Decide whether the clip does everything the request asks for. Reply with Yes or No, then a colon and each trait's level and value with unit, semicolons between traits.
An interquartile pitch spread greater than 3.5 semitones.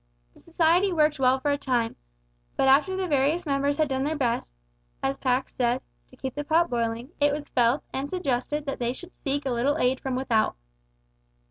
No: average, 3.2 semitones